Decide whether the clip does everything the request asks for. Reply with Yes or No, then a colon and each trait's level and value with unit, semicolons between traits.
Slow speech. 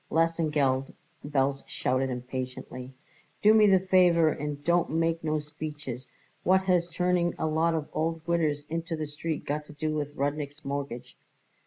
No: average, 155 wpm